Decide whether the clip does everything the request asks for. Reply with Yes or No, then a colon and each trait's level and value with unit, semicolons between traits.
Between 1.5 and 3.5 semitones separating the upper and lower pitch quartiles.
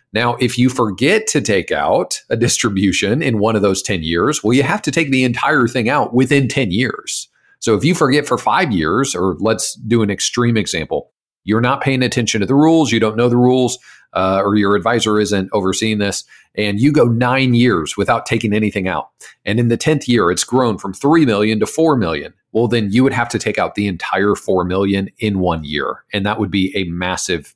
No: average, 3.9 semitones